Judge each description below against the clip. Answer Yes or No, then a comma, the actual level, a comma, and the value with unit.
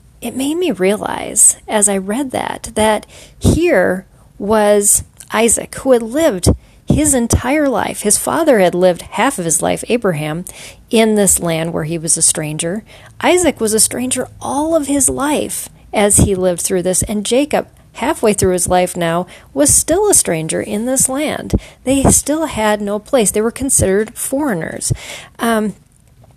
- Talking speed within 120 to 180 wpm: Yes, average, 165 wpm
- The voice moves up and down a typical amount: No, wide, 6.6 semitones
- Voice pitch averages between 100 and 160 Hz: No, high, 215 Hz